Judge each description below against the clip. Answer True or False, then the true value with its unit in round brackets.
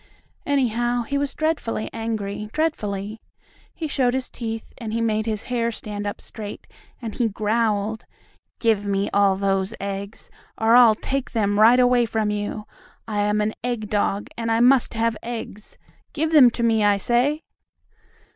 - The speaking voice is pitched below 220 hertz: False (225 Hz)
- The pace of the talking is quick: False (165 wpm)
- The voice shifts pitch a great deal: False (2.7 semitones)